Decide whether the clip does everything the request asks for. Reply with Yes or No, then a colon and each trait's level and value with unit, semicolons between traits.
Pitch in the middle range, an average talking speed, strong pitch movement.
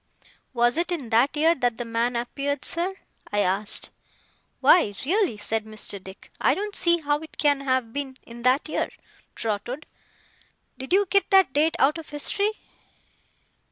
No: very high, 275 Hz; average, 160 wpm; wide, 6.0 semitones